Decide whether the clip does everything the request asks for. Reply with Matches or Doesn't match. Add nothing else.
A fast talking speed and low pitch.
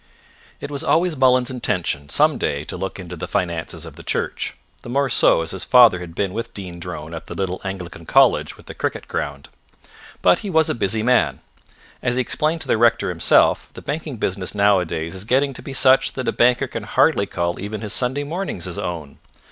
Matches